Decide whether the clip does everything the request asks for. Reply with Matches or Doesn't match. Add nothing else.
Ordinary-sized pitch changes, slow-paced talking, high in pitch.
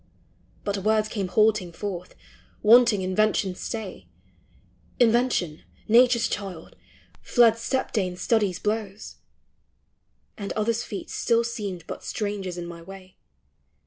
Matches